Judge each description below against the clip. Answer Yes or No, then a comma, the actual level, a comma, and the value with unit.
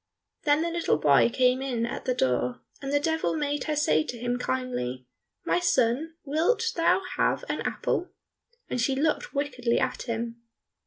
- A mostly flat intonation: No, average, 4.8 semitones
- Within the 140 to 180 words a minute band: Yes, average, 170 wpm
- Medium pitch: No, very high, 255 Hz